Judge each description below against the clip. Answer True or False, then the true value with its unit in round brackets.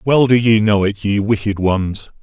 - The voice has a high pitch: False (105 Hz)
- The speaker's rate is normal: False (215 wpm)